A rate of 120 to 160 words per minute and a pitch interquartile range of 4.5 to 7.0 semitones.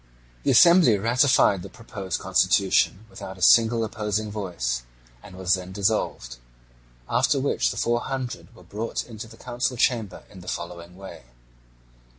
No: average, 150 wpm; average, 4.1 semitones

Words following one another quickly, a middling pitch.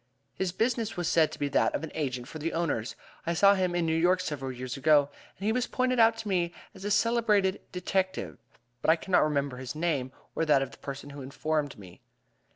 Yes: fast, 225 wpm; medium, 165 Hz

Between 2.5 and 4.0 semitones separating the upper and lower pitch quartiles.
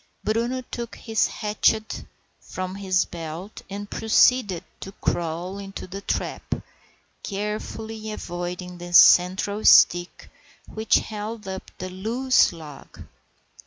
Yes: average, 3.3 semitones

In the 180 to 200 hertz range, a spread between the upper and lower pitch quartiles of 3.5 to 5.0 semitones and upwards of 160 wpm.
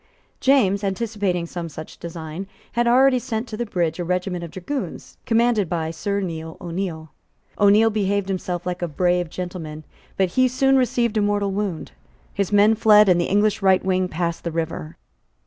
Yes: high, 190 Hz; average, 3.8 semitones; average, 175 wpm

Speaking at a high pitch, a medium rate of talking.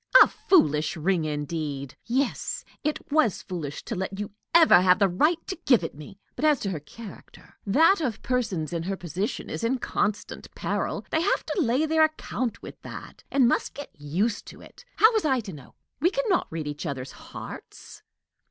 Yes: high, 205 Hz; average, 195 wpm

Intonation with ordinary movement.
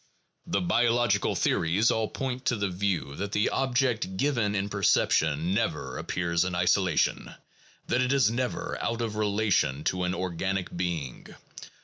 Yes: average, 4.6 semitones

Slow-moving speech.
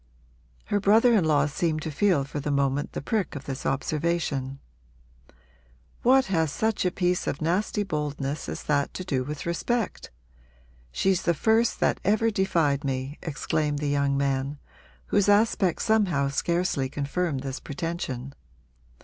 No: average, 150 wpm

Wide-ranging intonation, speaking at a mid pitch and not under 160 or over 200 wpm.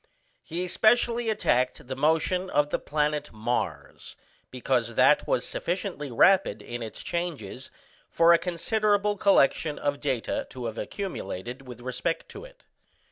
No: wide, 7.1 semitones; medium, 150 Hz; slow, 135 wpm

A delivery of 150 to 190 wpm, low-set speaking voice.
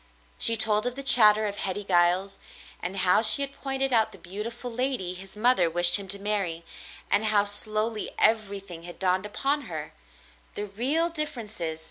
No: average, 180 wpm; high, 210 Hz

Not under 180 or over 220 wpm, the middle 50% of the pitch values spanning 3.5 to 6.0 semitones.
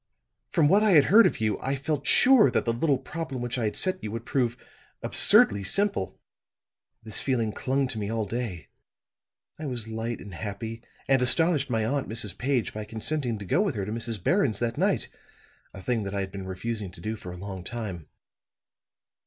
Yes: average, 200 wpm; average, 4.7 semitones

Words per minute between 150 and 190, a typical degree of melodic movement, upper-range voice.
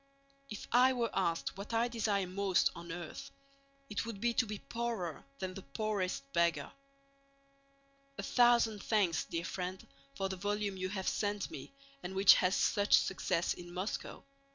Yes: average, 160 wpm; average, 3.2 semitones; high, 200 Hz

